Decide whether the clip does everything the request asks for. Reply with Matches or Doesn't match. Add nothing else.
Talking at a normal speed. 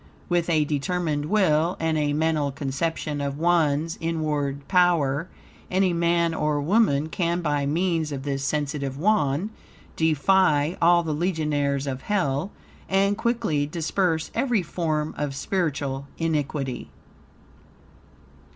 Doesn't match